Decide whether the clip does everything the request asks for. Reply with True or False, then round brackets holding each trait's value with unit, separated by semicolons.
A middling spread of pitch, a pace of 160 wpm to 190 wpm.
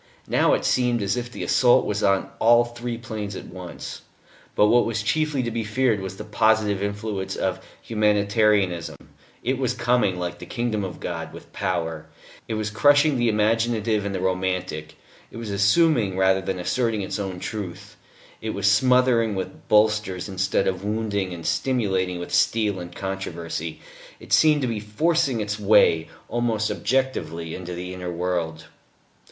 True (3.8 semitones; 165 wpm)